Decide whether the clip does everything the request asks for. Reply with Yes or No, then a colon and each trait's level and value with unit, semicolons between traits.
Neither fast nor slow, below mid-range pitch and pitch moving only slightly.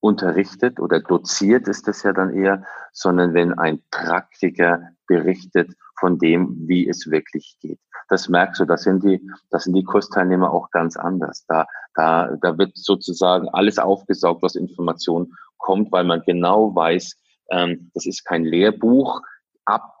Yes: average, 155 wpm; very low, 90 Hz; narrow, 2.0 semitones